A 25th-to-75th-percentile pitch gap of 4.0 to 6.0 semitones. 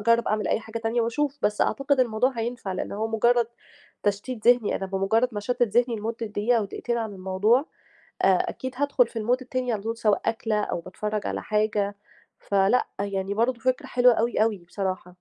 No: average, 2.9 semitones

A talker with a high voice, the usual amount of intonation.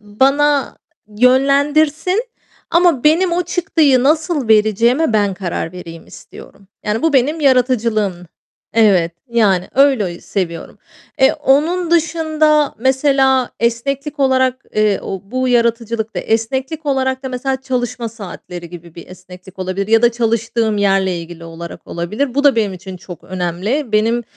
No: high, 240 Hz; wide, 5.8 semitones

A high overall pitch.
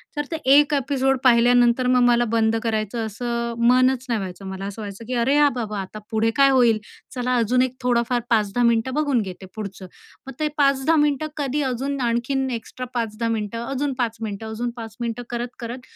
Yes: high, 240 Hz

